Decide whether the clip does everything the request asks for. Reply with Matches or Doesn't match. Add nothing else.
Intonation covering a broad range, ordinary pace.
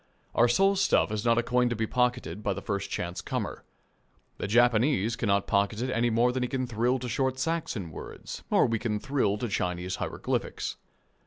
Doesn't match